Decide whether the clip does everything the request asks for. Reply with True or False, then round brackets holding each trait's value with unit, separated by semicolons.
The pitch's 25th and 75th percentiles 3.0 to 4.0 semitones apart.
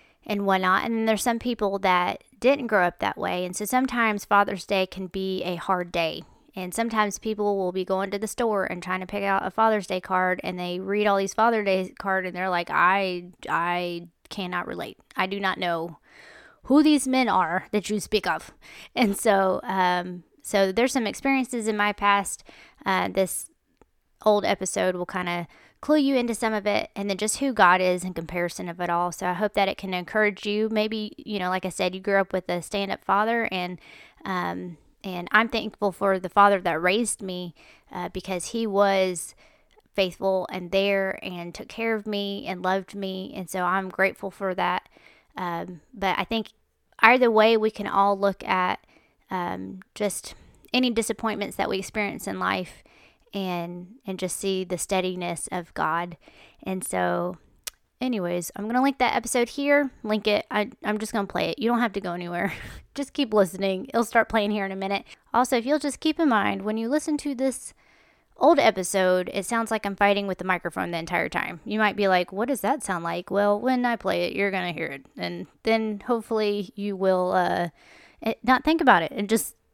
True (3.3 semitones)